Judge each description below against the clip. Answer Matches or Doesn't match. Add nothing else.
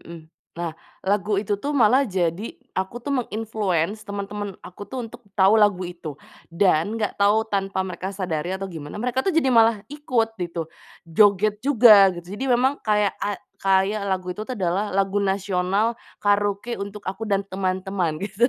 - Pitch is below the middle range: Doesn't match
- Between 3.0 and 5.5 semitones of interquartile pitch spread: Doesn't match